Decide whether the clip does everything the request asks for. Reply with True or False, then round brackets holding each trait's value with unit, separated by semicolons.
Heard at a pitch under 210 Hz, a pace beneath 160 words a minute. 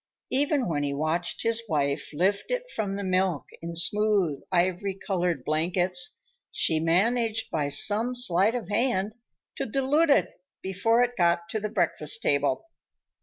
True (190 Hz; 150 wpm)